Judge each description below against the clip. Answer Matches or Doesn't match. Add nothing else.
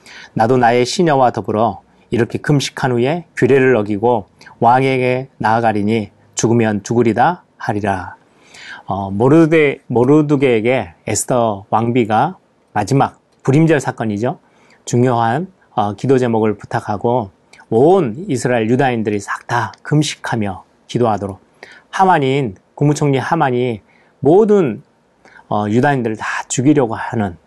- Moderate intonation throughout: Matches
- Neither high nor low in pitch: Doesn't match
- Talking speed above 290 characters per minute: Doesn't match